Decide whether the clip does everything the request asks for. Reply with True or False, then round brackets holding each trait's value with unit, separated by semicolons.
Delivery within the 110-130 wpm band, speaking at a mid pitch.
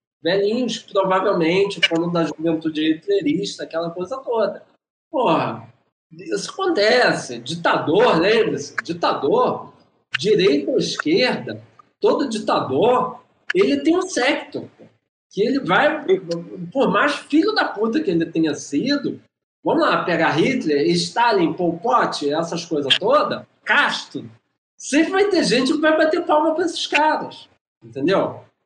False (125 wpm; 240 Hz)